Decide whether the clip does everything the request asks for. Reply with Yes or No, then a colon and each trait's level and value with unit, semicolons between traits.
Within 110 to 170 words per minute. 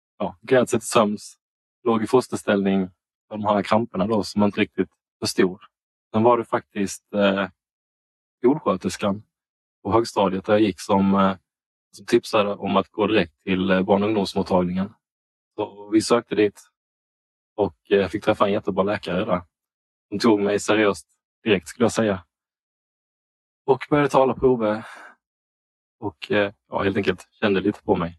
Yes: average, 160 wpm